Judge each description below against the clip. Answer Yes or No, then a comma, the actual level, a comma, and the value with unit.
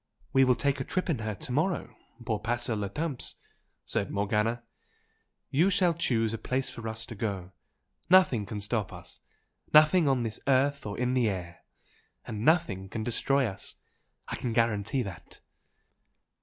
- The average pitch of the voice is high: No, low, 120 Hz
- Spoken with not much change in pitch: No, average, 4.5 semitones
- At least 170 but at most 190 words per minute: No, average, 160 wpm